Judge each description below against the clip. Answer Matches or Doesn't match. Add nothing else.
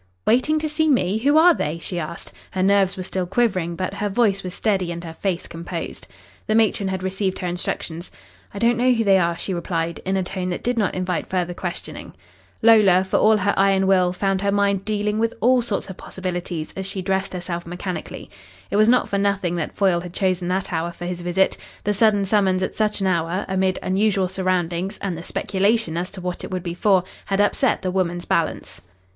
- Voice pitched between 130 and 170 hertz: Doesn't match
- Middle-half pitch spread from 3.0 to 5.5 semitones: Doesn't match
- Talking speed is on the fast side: Matches